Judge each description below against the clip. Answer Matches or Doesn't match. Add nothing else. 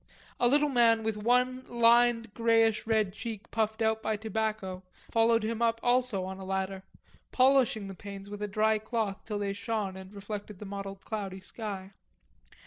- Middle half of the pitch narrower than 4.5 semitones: Matches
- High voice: Matches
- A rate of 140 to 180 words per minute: Matches